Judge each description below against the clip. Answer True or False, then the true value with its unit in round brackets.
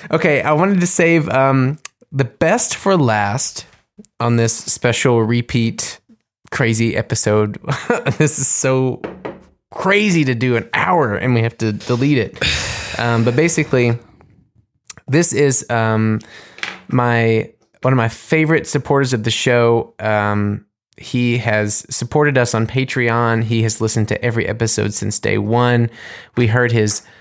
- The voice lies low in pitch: True (120 Hz)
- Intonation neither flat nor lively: True (3.6 semitones)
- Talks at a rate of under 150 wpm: True (140 wpm)